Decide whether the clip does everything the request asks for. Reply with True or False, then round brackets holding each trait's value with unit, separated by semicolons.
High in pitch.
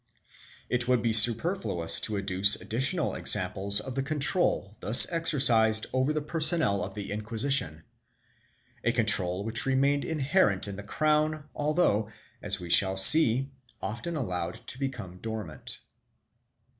False (115 Hz)